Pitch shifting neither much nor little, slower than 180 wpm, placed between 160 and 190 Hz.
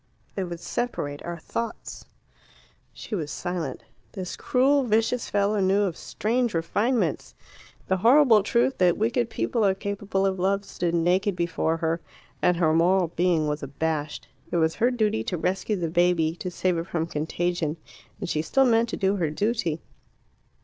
Yes: average, 4.4 semitones; average, 165 wpm; medium, 185 Hz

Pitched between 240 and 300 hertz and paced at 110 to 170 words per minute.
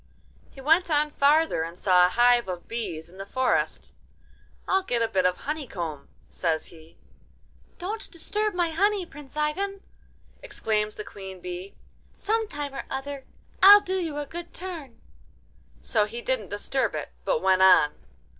Yes: very high, 265 Hz; average, 160 wpm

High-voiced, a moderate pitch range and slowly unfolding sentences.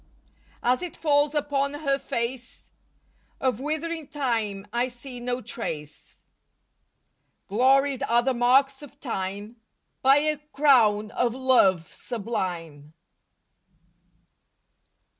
Yes: very high, 250 Hz; average, 4.4 semitones; slow, 100 wpm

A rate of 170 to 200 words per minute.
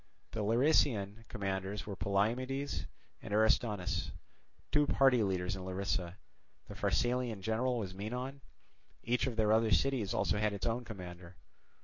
No: slow, 135 wpm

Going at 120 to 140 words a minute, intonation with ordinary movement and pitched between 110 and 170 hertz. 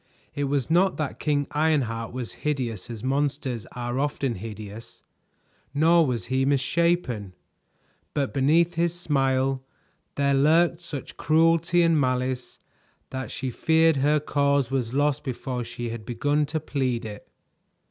Yes: slow, 135 wpm; average, 3.6 semitones; medium, 140 Hz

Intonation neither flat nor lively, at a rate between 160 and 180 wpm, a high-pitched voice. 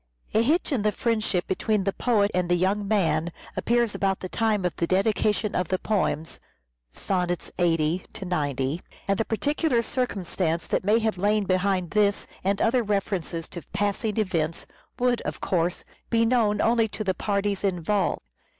Yes: average, 3.4 semitones; average, 165 wpm; high, 200 Hz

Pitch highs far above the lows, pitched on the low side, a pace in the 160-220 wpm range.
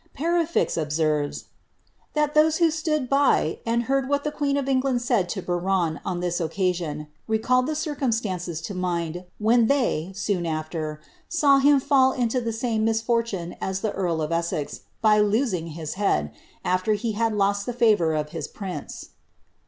No: wide, 7.2 semitones; high, 210 Hz; average, 170 wpm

